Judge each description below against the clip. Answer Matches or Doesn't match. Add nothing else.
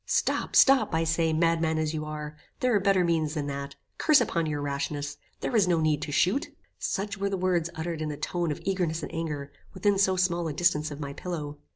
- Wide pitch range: Doesn't match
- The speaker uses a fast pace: Matches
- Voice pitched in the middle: Matches